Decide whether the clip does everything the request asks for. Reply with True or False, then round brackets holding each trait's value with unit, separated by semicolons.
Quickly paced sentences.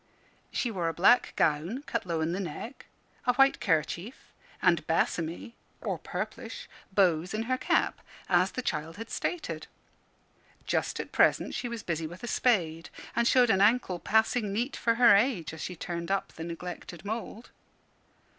False (165 wpm)